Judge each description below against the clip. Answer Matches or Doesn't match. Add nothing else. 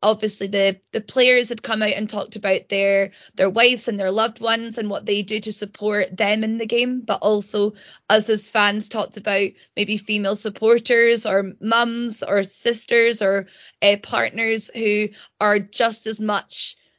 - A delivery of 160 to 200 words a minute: Matches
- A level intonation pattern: Matches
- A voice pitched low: Doesn't match